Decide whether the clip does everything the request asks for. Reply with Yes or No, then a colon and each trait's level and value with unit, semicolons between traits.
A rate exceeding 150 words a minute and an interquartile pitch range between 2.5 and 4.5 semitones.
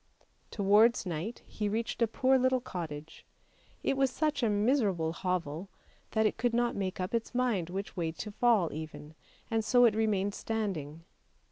No: average, 165 wpm; average, 5.1 semitones